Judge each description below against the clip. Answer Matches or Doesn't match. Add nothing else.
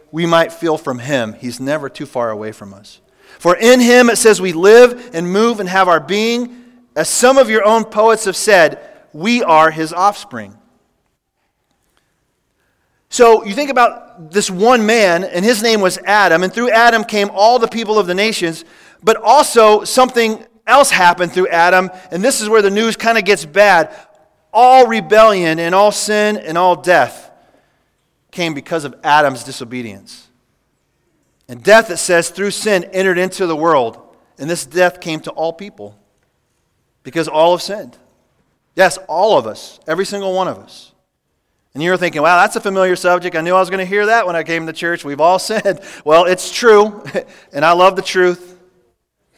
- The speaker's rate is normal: Matches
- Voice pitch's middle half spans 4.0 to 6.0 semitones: Matches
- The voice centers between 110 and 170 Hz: Doesn't match